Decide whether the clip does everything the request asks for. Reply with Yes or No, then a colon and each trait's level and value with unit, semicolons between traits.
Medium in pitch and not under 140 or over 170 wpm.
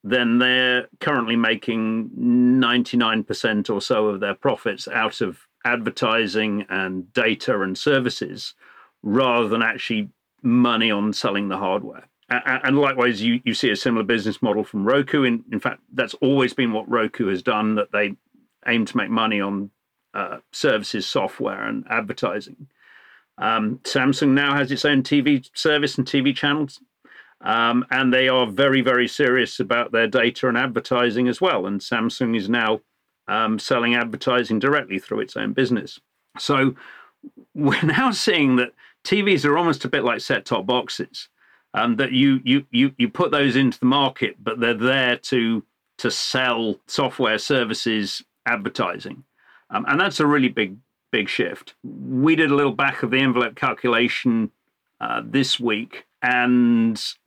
No: low, 125 Hz; average, 160 wpm